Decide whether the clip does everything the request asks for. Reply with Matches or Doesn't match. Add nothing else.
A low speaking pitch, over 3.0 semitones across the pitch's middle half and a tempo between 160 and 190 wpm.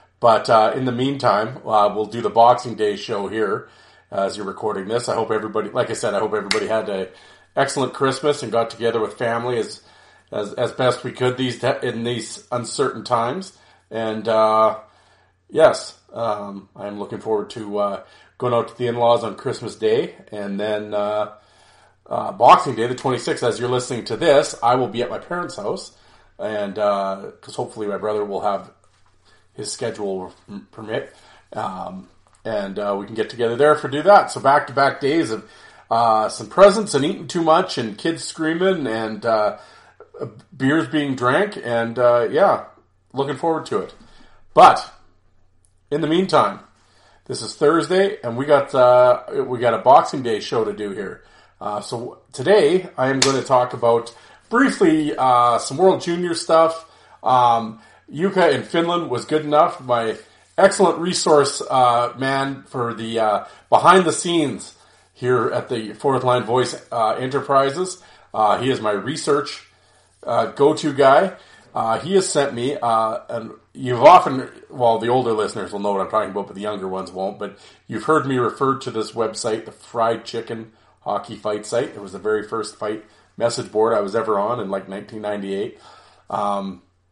Matches